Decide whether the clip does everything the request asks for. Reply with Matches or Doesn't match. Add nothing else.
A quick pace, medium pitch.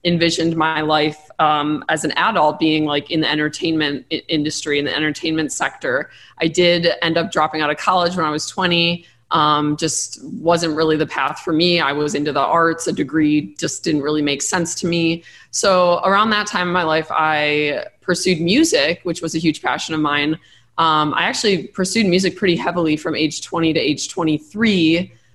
Doesn't match